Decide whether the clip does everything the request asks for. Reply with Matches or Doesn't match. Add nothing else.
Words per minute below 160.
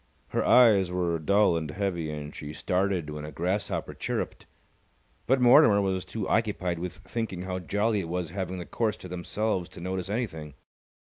Doesn't match